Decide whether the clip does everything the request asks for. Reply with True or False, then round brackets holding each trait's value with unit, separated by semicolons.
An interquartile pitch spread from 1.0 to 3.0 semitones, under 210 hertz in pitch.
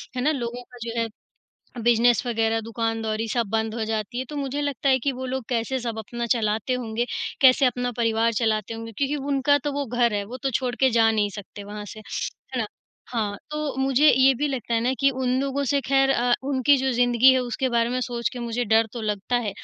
False (2.7 semitones; 240 Hz)